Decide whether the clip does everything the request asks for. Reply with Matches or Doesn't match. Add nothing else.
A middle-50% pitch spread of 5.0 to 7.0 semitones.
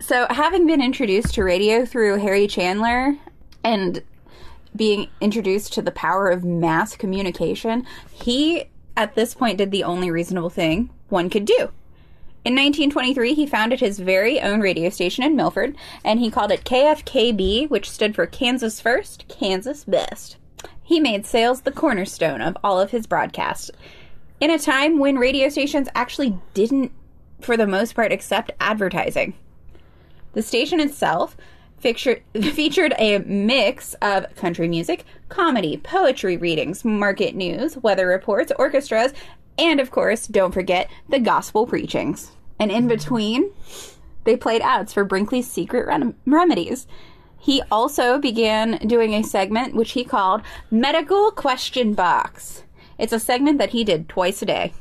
Matches